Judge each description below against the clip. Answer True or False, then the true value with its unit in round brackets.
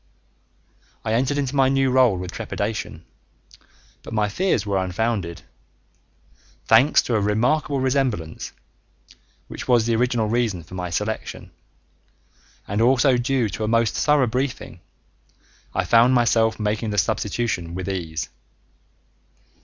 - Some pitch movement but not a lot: True (4.1 semitones)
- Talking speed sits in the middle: False (130 wpm)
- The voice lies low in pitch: True (115 Hz)